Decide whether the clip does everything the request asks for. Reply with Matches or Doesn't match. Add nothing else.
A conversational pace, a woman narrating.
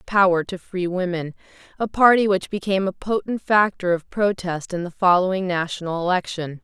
Matches